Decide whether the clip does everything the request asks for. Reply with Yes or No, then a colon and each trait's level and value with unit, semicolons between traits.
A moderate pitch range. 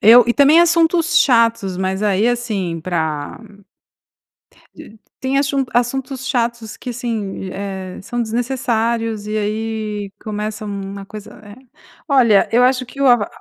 Yes: average, 3.4 semitones